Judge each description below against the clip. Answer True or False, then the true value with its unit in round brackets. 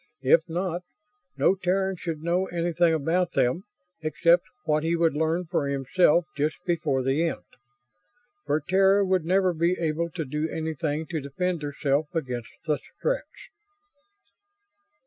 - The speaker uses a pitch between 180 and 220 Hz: False (165 Hz)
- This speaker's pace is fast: False (140 wpm)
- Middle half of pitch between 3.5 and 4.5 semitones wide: False (2.8 semitones)